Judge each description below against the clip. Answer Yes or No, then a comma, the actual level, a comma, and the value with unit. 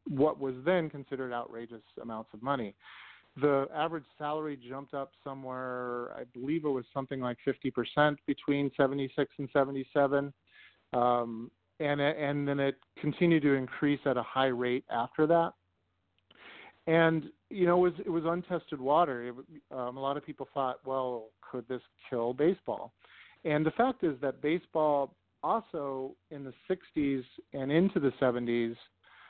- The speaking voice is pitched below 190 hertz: Yes, medium, 140 Hz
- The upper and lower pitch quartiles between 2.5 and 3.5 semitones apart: Yes, average, 3.2 semitones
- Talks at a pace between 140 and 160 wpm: Yes, average, 150 wpm